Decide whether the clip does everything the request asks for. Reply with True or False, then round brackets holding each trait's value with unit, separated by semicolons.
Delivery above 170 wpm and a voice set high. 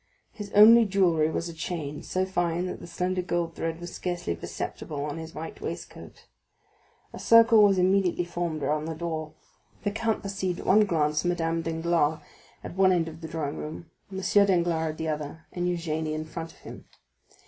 False (185 wpm; 170 Hz)